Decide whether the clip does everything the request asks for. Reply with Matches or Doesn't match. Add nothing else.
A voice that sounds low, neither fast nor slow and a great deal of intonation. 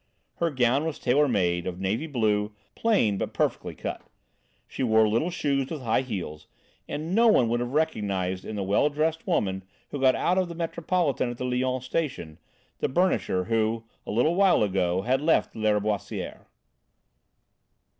Matches